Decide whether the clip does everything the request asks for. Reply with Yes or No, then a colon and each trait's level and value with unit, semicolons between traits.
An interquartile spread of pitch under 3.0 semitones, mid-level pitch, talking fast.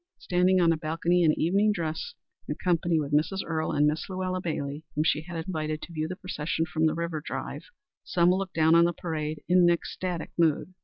Yes: narrow, 2.4 semitones; medium, 165 Hz; fast, 210 wpm